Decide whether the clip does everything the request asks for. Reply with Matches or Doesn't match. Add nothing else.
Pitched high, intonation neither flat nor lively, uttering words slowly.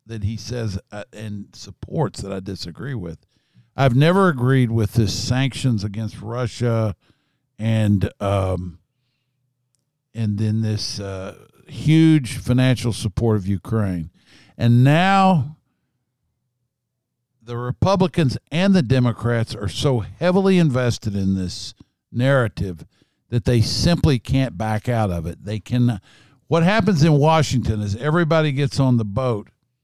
Doesn't match